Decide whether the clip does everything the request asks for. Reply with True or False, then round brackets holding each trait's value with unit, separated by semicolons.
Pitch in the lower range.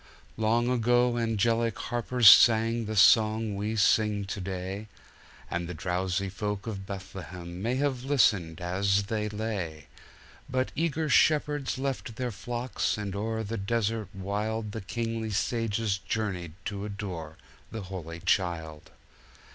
True (105 Hz)